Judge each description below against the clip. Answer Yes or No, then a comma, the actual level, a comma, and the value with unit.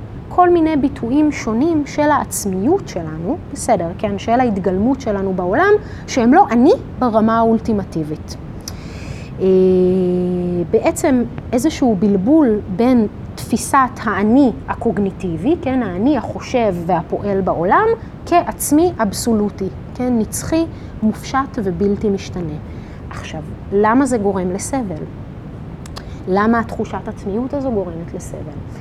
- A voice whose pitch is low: No, high, 220 Hz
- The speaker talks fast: No, slow, 100 wpm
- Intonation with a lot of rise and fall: Yes, wide, 6.0 semitones